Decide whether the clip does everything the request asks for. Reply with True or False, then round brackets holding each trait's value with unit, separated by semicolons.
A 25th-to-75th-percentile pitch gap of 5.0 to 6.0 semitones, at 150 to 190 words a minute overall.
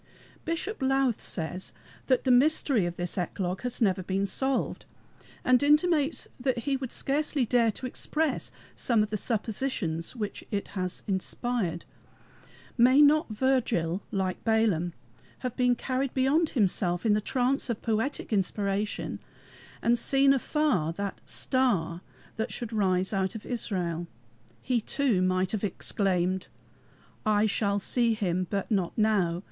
False (5.6 semitones; 140 wpm)